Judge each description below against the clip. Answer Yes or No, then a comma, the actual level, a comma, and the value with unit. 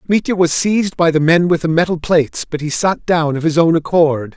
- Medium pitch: Yes, medium, 165 Hz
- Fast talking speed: Yes, fast, 250 wpm